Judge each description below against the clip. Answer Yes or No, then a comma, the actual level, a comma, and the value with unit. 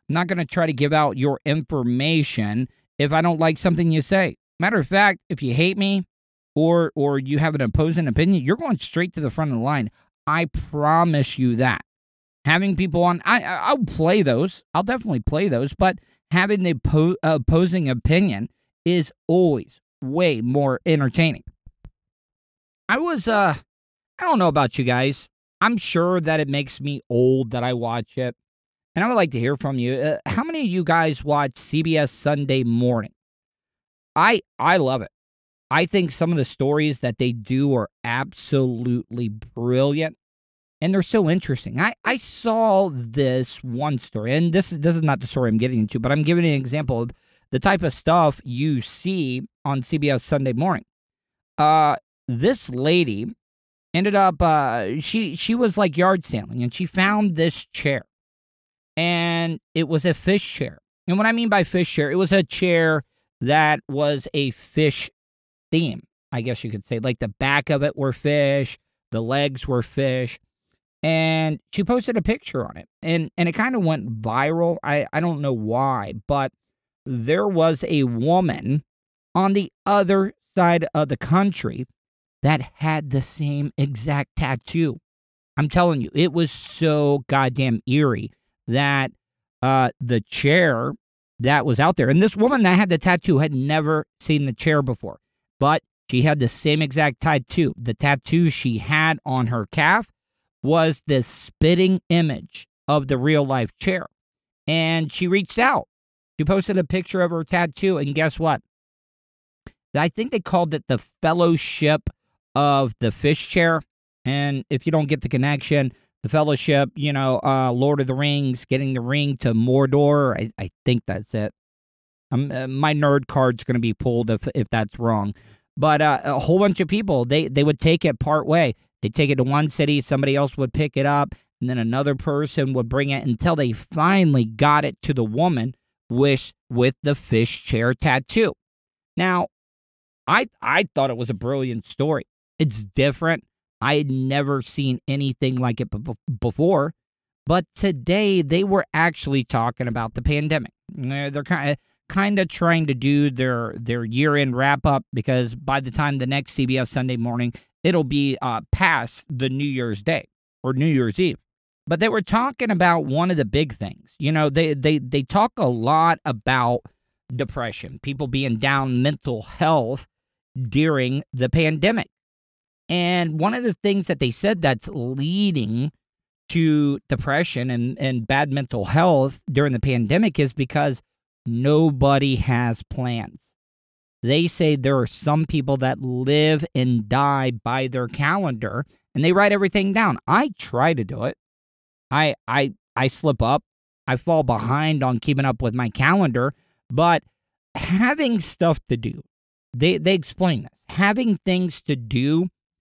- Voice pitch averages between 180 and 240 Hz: No, medium, 145 Hz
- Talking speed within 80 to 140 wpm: No, average, 170 wpm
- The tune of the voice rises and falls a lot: No, average, 4.6 semitones